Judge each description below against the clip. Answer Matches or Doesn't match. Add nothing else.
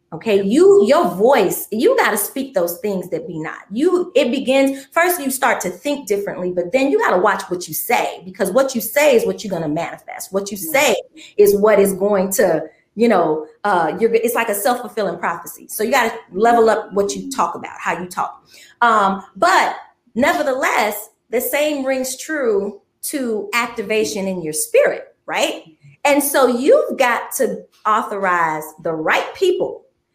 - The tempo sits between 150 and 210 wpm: Matches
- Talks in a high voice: Matches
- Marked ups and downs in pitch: Matches